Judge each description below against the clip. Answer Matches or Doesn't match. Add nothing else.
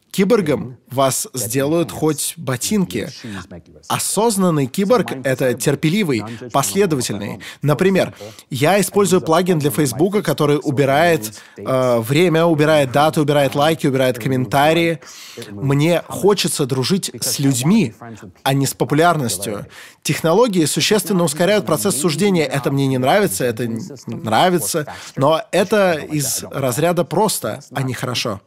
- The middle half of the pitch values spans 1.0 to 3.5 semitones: Doesn't match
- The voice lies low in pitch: Doesn't match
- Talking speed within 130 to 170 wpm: Doesn't match